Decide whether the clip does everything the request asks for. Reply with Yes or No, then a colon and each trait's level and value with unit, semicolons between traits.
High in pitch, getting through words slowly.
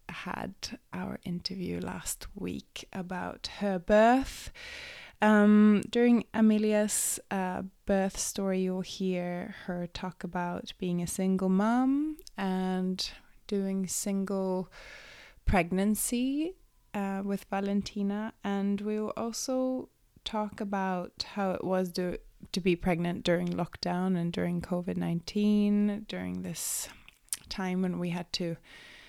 Yes: high, 195 Hz; slow, 115 wpm